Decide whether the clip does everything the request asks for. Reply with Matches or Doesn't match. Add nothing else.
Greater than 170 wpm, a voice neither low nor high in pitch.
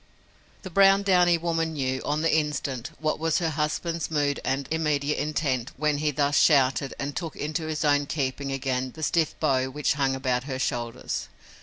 Matches